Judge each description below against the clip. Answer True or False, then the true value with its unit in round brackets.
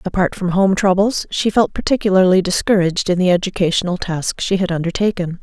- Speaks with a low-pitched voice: False (185 Hz)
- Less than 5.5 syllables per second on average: False (5.9 syllables/s)